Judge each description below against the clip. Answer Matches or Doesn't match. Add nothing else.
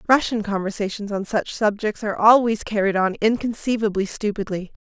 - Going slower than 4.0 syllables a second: Doesn't match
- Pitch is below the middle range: Doesn't match